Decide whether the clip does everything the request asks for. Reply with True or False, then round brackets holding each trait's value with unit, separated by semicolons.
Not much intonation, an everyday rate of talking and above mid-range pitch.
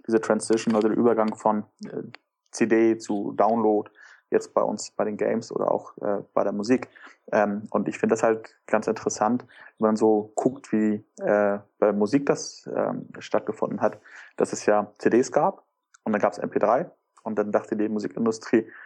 False (1.2 semitones; 180 wpm; 110 Hz)